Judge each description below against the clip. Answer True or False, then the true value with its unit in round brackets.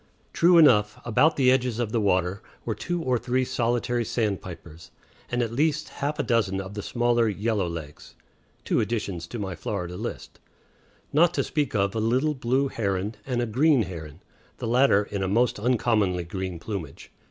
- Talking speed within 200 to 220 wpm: False (170 wpm)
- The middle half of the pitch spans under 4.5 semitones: False (4.8 semitones)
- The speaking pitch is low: True (115 Hz)